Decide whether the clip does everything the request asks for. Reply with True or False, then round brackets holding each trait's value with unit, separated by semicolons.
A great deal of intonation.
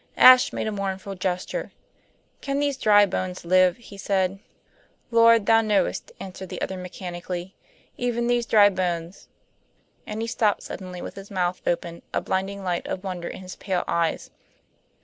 False (3.0 semitones)